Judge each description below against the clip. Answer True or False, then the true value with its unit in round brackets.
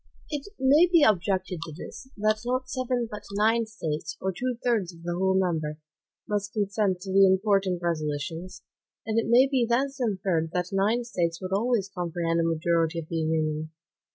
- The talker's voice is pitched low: False (190 Hz)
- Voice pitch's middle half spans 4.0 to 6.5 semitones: True (5.3 semitones)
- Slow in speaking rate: False (180 wpm)